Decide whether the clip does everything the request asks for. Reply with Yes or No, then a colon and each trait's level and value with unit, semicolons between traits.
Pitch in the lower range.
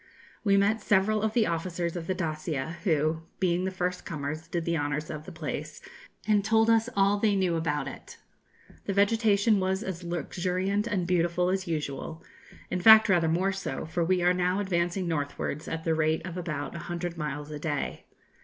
No: medium, 175 Hz